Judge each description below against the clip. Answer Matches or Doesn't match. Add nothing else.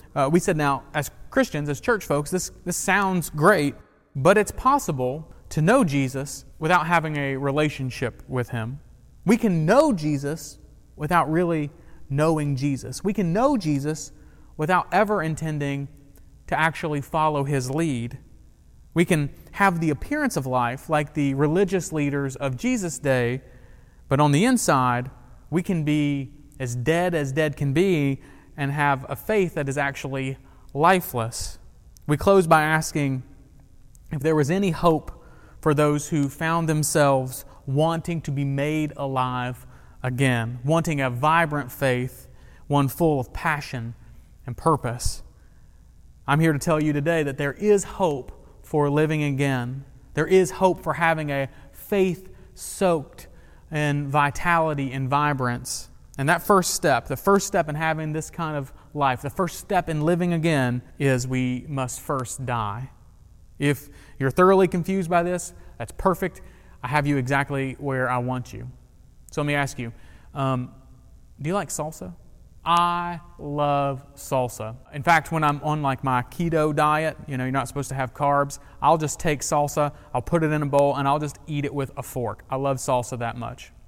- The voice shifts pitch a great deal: Doesn't match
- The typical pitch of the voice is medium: Matches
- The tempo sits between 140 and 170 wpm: Matches